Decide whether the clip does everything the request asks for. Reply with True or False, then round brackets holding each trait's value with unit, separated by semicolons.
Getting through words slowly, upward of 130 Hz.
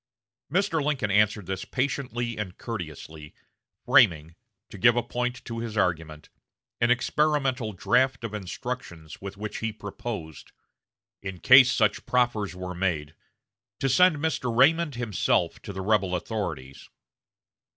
False (130 wpm; 110 Hz)